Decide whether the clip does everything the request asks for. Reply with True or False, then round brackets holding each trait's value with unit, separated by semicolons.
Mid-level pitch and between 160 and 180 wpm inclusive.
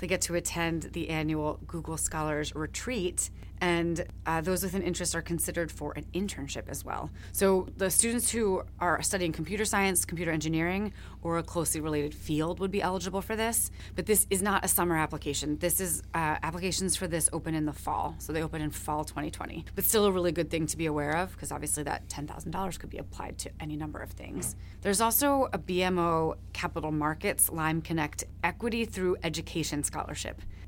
False (170 Hz; 195 wpm)